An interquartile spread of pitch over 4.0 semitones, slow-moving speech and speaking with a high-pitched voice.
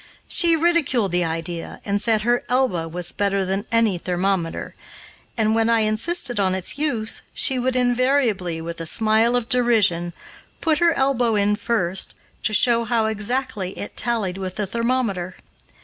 No: average, 4.6 semitones; average, 160 wpm; high, 220 Hz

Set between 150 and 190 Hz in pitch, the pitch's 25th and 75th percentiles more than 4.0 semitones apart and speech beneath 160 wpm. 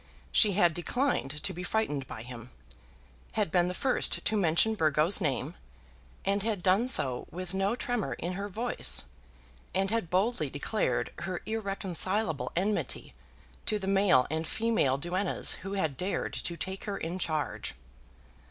Yes: medium, 185 Hz; average, 4.6 semitones; average, 150 wpm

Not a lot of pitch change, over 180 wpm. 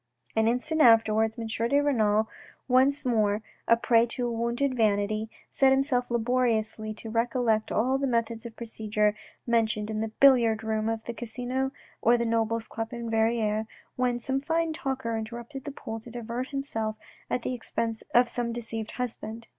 No: narrow, 2.1 semitones; average, 165 wpm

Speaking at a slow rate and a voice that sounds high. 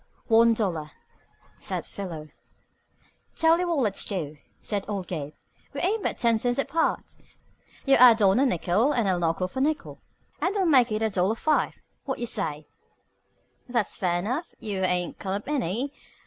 No: average, 170 wpm; high, 220 Hz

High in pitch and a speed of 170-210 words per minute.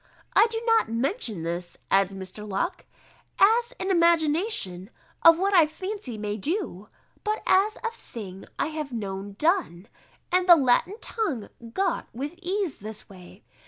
No: very high, 305 Hz; average, 155 wpm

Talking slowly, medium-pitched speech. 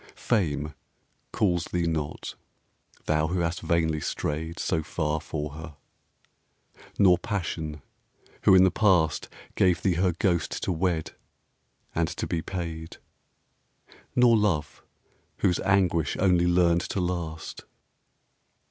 No: slow, 120 wpm; very low, 85 Hz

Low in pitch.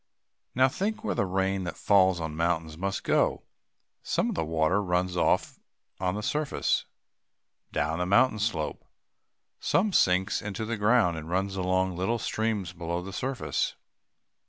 Yes: very low, 95 Hz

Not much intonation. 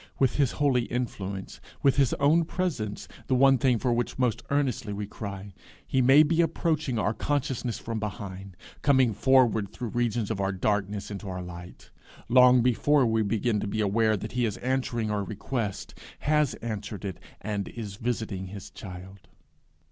No: average, 4.3 semitones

